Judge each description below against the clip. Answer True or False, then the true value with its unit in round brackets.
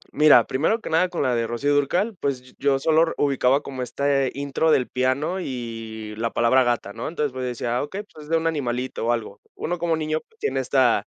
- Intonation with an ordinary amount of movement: True (4.2 semitones)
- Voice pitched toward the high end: False (140 Hz)